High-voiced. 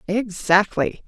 Yes: high, 195 Hz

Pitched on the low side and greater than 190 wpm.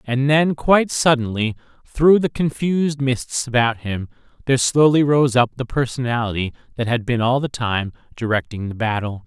No: low, 125 Hz; average, 160 wpm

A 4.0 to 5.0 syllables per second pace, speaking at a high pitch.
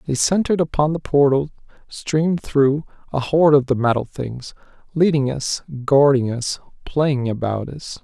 No: 4.7 syllables/s; medium, 140 Hz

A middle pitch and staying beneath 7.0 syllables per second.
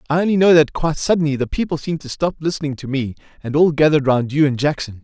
No: medium, 150 Hz; 7.1 syllables/s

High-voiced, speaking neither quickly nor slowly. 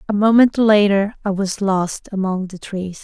Yes: high, 200 Hz; average, 180 wpm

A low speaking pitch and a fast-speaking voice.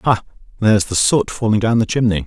Yes: low, 105 Hz; fast, 210 wpm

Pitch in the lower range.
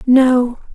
No: very high, 250 Hz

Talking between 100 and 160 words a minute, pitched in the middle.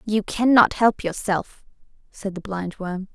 No: slow, 135 wpm; high, 200 Hz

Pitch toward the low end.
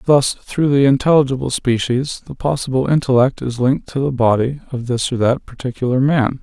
Yes: low, 130 Hz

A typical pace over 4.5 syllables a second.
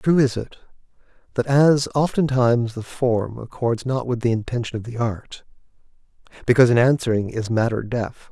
Yes: 5.1 syllables/s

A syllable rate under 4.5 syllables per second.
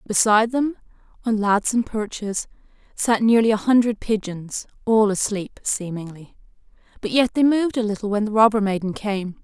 No: 5.0 syllables/s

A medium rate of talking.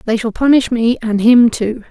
No: fast, 220 wpm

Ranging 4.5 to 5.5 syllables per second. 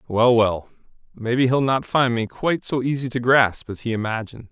Yes: 5.4 syllables/s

